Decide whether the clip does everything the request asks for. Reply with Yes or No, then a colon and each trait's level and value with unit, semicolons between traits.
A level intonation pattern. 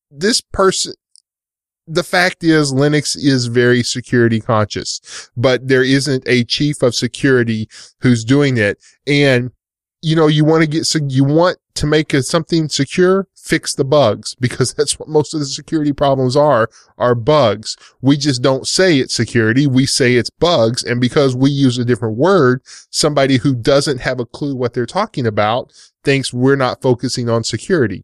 No: average, 3.6 semitones